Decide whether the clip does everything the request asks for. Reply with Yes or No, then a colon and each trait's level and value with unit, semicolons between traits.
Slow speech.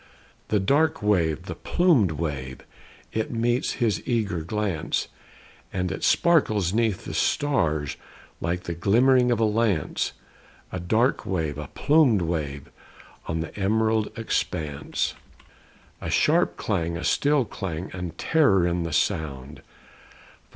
Yes: slow, 130 wpm